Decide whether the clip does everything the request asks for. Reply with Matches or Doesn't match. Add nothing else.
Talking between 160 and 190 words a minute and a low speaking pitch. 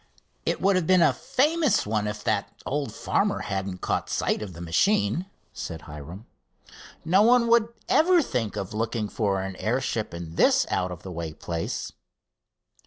Matches